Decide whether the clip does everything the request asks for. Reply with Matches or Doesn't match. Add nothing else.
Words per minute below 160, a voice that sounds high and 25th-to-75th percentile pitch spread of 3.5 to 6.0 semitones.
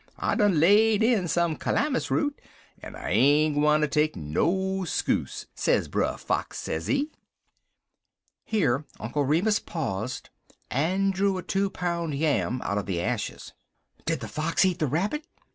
Doesn't match